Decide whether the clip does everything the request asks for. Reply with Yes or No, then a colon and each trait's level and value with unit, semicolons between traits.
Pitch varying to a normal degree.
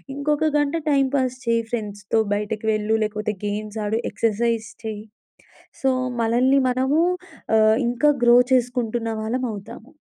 Yes: average, 3.1 semitones